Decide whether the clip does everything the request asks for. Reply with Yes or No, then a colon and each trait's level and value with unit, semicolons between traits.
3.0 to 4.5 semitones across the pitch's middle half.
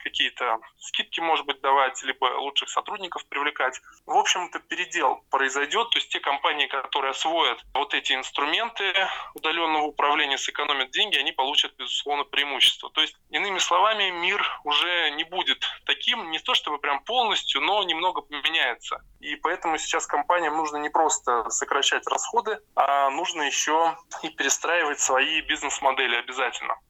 No: narrow, 2.5 semitones